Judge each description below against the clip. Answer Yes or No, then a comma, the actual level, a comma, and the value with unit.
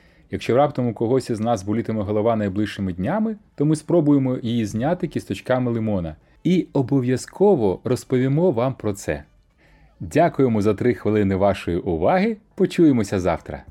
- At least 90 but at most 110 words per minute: No, average, 135 wpm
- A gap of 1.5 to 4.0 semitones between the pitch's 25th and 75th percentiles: No, average, 5.3 semitones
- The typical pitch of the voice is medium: No, low, 120 Hz